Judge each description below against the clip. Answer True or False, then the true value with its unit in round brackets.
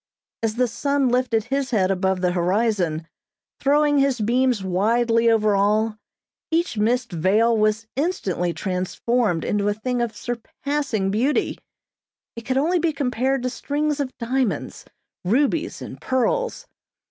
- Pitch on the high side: True (235 Hz)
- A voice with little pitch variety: False (4.6 semitones)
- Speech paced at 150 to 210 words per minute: False (135 wpm)